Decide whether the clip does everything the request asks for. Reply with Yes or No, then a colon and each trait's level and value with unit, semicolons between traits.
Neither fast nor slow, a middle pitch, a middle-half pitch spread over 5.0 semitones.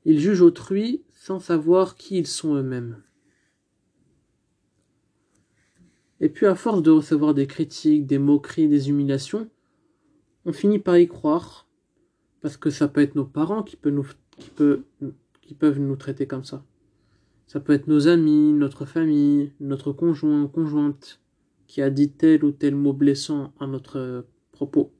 No: average, 155 wpm; medium, 150 Hz; average, 3.1 semitones